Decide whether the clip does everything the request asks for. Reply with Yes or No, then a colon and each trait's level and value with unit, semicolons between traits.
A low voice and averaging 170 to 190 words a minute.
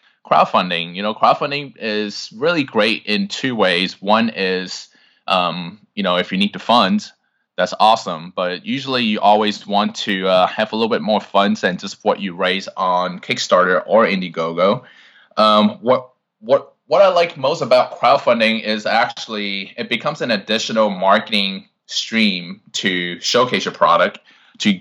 No: low, 110 Hz; average, 160 wpm